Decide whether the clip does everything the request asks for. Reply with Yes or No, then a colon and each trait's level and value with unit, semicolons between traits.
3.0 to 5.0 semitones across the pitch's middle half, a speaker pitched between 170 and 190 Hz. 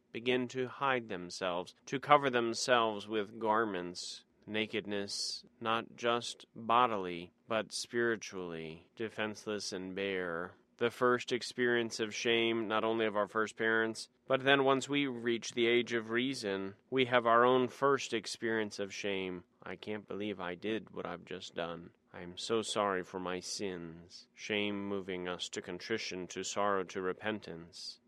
No: average, 3.9 semitones; low, 110 Hz